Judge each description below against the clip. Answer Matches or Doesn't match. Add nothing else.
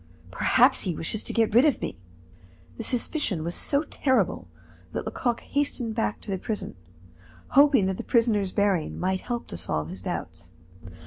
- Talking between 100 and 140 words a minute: Doesn't match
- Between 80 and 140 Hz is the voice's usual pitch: Doesn't match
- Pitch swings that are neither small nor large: Doesn't match